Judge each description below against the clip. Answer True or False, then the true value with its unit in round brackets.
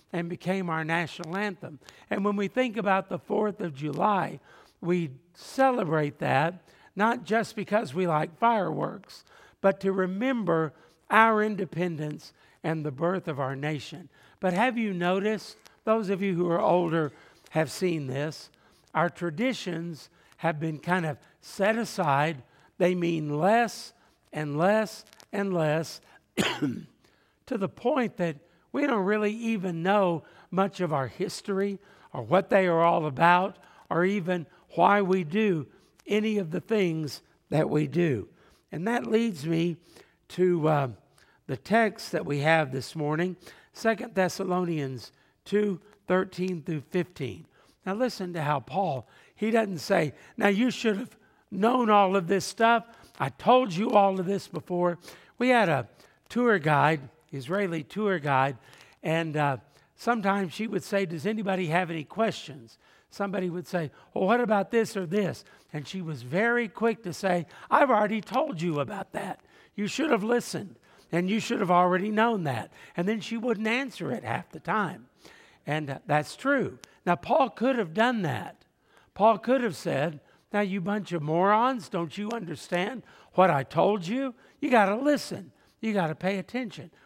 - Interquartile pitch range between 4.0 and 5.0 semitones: True (4.7 semitones)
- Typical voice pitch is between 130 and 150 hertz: False (185 Hz)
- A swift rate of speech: False (160 wpm)